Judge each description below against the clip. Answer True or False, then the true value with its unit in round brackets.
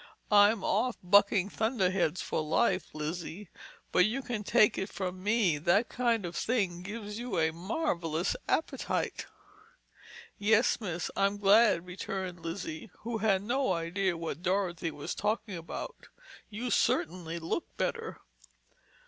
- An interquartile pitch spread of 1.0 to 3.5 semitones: False (4.2 semitones)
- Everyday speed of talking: False (130 wpm)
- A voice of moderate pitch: False (195 Hz)